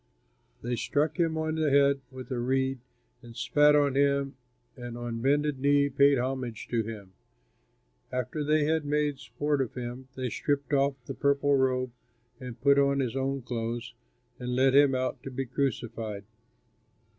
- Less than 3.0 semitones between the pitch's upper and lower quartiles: Yes, narrow, 2.4 semitones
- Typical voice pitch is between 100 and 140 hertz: Yes, low, 135 Hz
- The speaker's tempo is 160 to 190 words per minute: Yes, average, 165 wpm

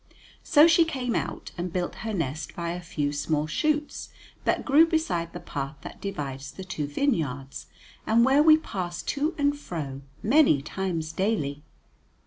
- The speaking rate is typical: Yes, average, 160 wpm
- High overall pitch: No, medium, 180 Hz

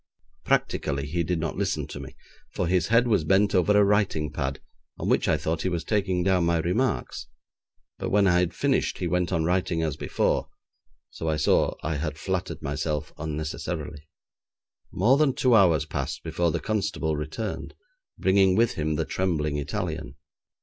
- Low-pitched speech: Yes, very low, 85 Hz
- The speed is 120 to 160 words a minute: No, average, 175 wpm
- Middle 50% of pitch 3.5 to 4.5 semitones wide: Yes, average, 3.8 semitones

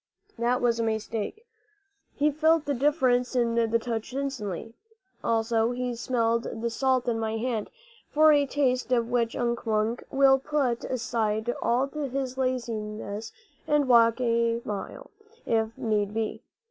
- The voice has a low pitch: No, high, 235 Hz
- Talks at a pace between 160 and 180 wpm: No, average, 145 wpm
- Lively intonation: No, narrow, 2.6 semitones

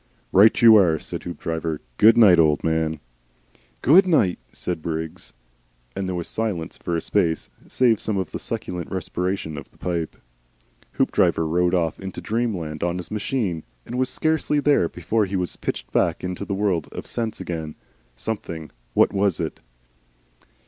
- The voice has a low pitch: Yes, very low, 90 Hz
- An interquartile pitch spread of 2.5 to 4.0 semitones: No, average, 4.7 semitones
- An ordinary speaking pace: Yes, average, 160 wpm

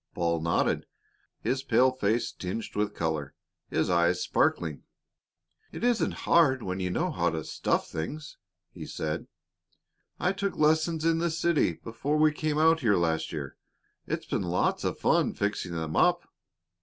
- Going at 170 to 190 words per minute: No, average, 155 wpm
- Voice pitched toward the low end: Yes, low, 110 Hz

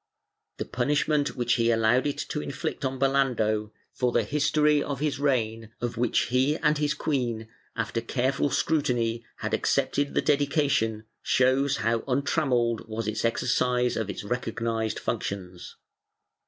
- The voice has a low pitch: Yes, low, 125 Hz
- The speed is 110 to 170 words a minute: Yes, average, 140 wpm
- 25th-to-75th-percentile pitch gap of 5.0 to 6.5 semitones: No, average, 3.7 semitones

